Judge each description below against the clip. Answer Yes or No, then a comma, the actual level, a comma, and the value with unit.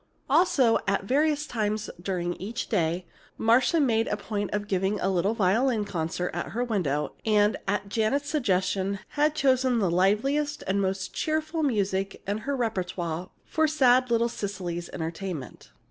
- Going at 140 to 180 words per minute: Yes, average, 150 wpm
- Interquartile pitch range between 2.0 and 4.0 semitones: No, average, 5.3 semitones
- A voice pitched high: Yes, high, 210 Hz